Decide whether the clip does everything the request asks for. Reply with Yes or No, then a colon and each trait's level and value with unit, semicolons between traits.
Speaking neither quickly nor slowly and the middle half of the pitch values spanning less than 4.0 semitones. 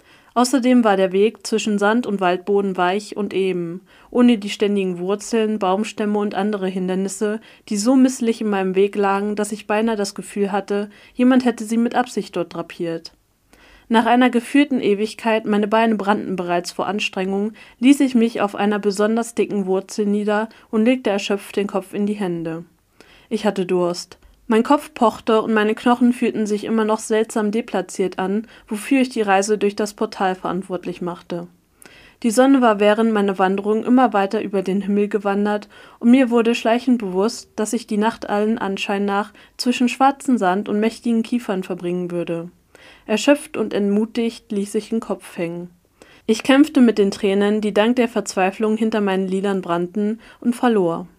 Yes: average, 170 wpm; average, 2.7 semitones